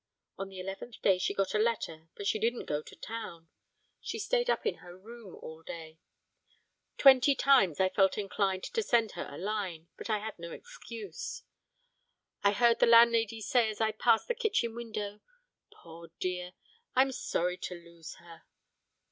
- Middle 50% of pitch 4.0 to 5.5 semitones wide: Yes, average, 4.6 semitones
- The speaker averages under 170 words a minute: No, average, 175 wpm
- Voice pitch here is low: No, high, 205 Hz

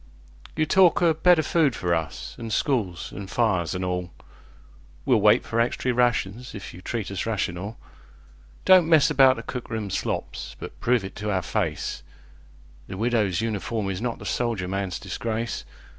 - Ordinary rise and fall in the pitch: Yes, average, 4.8 semitones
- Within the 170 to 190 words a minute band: No, average, 160 wpm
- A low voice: Yes, low, 110 Hz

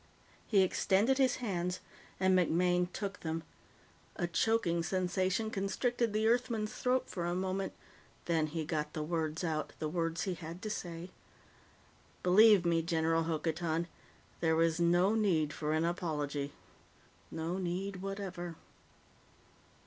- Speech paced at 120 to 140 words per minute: Yes, slow, 135 wpm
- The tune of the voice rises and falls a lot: No, average, 3.1 semitones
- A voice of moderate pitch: Yes, medium, 175 Hz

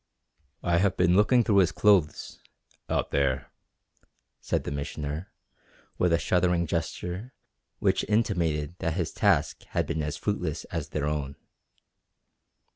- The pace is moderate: No, slow, 130 wpm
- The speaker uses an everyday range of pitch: Yes, average, 4.0 semitones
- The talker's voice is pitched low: Yes, very low, 85 Hz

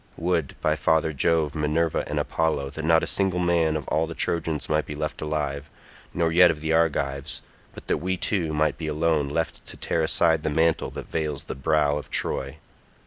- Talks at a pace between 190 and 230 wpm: Yes, average, 200 wpm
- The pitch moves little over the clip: Yes, narrow, 1.6 semitones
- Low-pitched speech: Yes, very low, 80 Hz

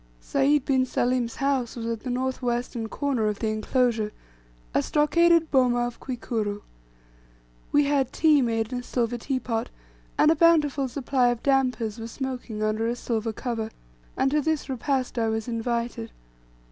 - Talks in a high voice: Yes, high, 245 Hz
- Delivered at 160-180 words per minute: Yes, average, 165 wpm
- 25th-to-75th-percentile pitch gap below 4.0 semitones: Yes, average, 3.1 semitones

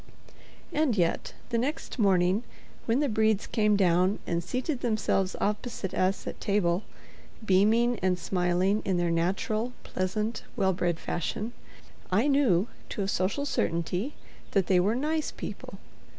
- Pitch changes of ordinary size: Yes, average, 4.2 semitones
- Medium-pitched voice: No, high, 200 Hz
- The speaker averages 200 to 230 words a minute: No, average, 140 wpm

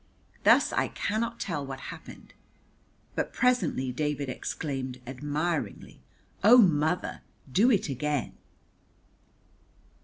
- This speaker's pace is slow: Yes, slow, 95 wpm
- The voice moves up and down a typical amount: No, wide, 6.4 semitones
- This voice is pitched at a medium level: Yes, medium, 150 Hz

